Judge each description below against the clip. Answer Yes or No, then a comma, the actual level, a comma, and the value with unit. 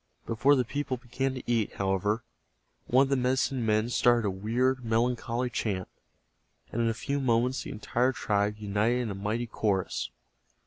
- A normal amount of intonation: Yes, average, 3.0 semitones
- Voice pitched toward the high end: No, low, 120 Hz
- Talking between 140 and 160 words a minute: No, average, 170 wpm